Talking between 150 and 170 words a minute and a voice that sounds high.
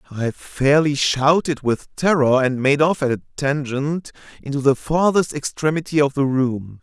No: average, 160 wpm; medium, 140 Hz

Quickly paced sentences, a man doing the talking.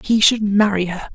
No: fast, 210 wpm; female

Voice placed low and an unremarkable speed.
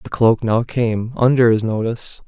Yes: low, 115 Hz; average, 185 wpm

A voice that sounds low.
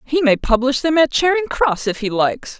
No: very high, 275 Hz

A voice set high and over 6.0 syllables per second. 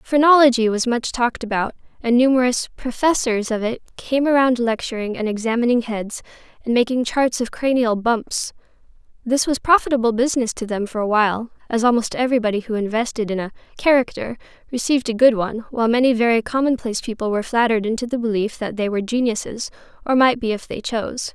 Yes: high, 235 Hz; 6.2 syllables/s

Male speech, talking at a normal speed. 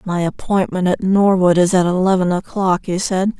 No: female; average, 175 wpm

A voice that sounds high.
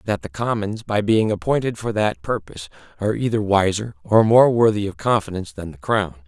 No: low, 105 Hz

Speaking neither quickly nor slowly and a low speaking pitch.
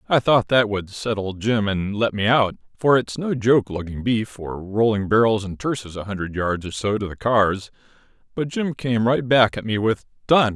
No: fast, 215 wpm; low, 110 Hz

